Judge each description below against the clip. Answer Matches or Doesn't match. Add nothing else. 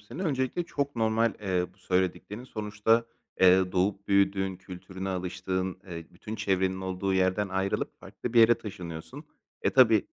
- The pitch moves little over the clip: Doesn't match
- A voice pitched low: Matches